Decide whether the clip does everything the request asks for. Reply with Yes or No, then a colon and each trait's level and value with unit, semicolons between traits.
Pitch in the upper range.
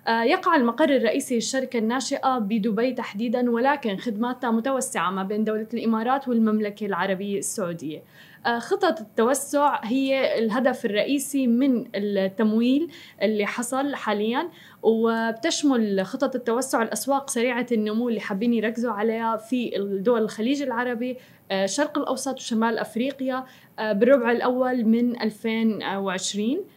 Yes: high, 235 Hz